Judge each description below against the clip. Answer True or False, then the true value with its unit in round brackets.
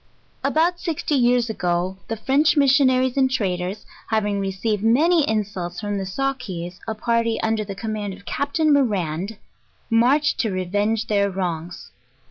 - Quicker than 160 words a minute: False (150 wpm)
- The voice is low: False (220 Hz)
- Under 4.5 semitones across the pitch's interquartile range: False (5.2 semitones)